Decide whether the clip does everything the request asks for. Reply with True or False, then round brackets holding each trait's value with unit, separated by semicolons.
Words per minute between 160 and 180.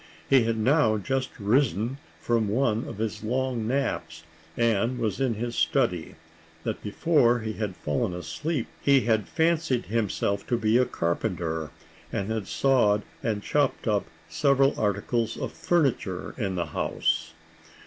False (145 wpm)